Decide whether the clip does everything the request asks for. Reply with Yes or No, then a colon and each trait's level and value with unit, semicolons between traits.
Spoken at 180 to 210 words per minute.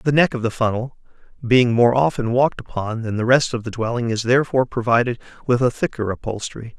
Yes: fast, 205 wpm